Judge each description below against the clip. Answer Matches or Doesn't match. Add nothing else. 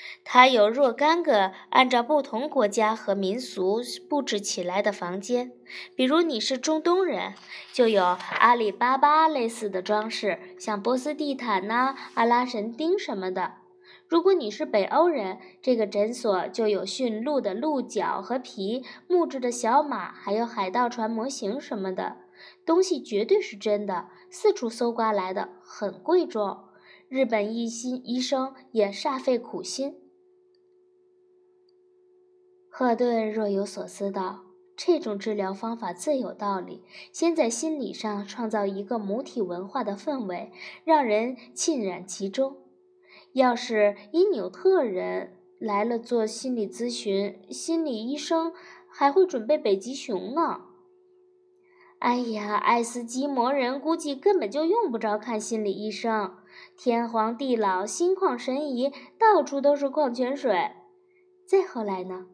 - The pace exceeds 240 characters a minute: Doesn't match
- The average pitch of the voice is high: Matches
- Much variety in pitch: Matches